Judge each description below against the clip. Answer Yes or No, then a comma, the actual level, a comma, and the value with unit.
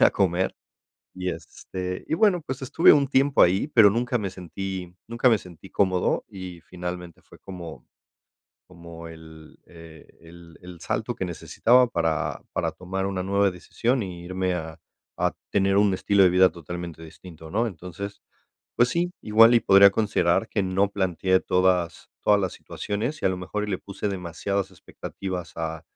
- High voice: No, very low, 95 Hz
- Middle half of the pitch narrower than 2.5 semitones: No, average, 2.8 semitones